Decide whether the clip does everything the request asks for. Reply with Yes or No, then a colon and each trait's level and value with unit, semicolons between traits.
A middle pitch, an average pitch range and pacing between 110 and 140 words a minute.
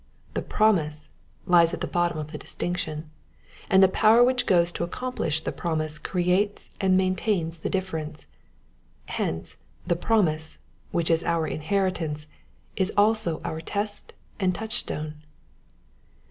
Yes: medium, 175 Hz; average, 3.8 semitones; slow, 135 wpm